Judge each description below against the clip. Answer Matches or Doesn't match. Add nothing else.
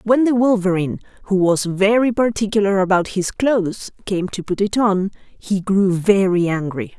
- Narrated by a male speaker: Doesn't match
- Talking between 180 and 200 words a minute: Doesn't match